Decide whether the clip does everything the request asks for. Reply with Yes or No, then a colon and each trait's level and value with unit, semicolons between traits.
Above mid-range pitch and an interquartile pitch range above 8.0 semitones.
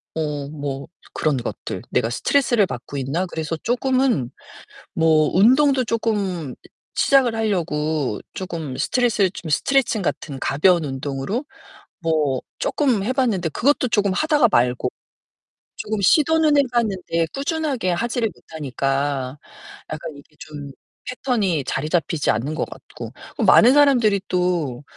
No: medium, 180 Hz; wide, 8.6 semitones